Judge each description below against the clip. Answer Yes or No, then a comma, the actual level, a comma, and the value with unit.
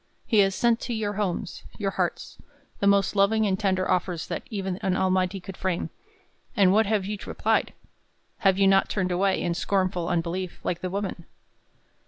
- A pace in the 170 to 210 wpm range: Yes, average, 180 wpm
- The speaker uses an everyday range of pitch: No, narrow, 1.7 semitones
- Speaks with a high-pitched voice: Yes, high, 195 Hz